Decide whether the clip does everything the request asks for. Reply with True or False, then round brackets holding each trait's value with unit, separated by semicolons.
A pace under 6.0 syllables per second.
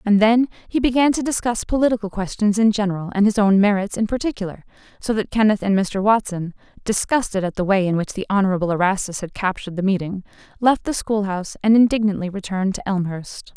False (6.2 syllables/s)